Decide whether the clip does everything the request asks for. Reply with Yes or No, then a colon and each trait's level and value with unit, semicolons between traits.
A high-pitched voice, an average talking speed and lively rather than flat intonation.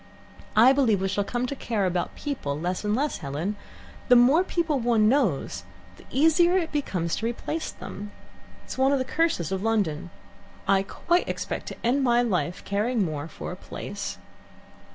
Yes: high, 225 Hz; average, 175 wpm; wide, 6.4 semitones